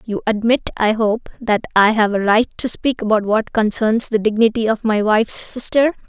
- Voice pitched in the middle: No, high, 220 Hz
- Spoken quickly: No, average, 195 wpm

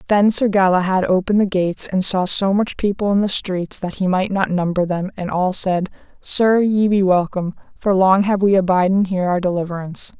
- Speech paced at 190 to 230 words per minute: Yes, fast, 205 wpm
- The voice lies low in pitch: No, high, 190 Hz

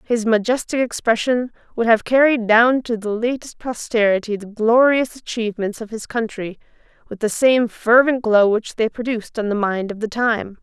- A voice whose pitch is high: Yes, high, 225 Hz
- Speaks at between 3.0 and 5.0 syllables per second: Yes, 4.9 syllables/s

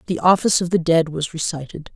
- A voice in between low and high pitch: Yes, medium, 165 Hz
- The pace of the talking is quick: Yes, fast, 215 wpm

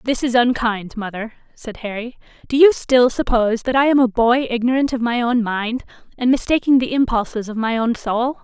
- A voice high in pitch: Yes, high, 240 Hz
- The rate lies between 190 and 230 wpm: Yes, average, 200 wpm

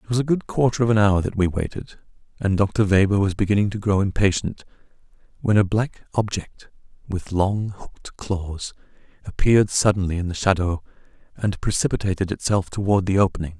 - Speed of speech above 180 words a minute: No, average, 170 wpm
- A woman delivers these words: No, male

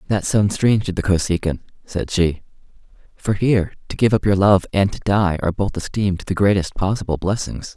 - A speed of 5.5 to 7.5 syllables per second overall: Yes, 5.7 syllables/s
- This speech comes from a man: Yes, male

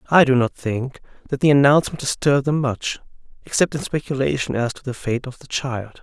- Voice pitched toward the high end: No, low, 130 Hz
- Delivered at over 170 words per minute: Yes, average, 200 wpm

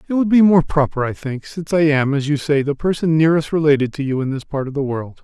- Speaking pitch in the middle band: Yes, medium, 150 Hz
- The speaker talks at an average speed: No, fast, 285 wpm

